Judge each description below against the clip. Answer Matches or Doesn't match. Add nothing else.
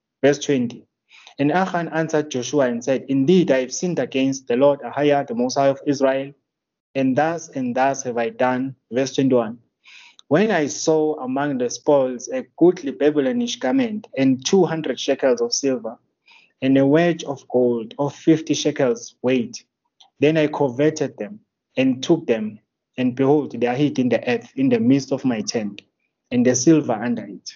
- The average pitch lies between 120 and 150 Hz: Matches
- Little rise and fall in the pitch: Doesn't match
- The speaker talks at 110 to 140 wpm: Doesn't match